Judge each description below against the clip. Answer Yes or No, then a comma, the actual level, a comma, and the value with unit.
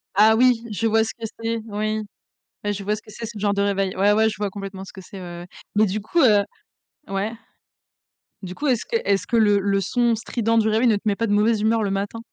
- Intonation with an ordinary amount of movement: No, narrow, 2.1 semitones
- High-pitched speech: Yes, high, 210 Hz